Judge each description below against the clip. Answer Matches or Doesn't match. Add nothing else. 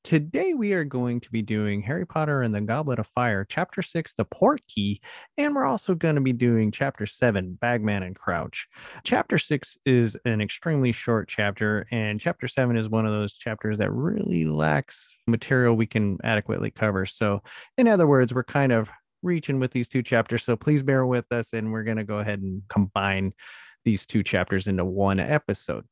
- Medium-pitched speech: Doesn't match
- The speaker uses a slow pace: Doesn't match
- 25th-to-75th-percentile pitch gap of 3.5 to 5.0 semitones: Matches